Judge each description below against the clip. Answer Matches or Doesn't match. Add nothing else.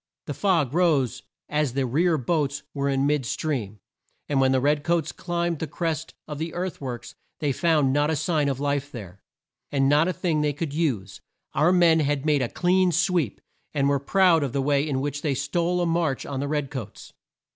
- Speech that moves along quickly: Matches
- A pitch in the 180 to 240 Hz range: Doesn't match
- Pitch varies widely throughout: Doesn't match